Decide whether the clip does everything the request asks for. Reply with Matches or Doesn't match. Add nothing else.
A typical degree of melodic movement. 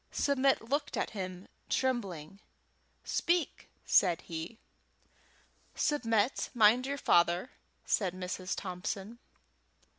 Doesn't match